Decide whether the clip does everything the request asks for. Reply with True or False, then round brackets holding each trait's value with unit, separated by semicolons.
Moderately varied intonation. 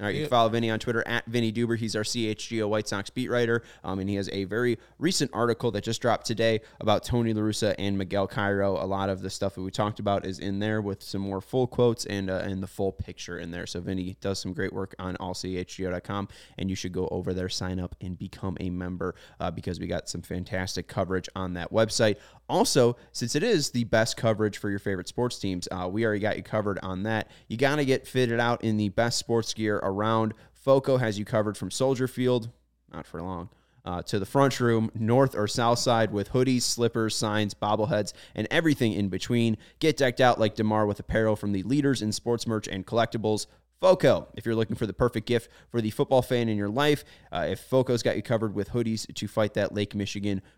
True (3.3 semitones)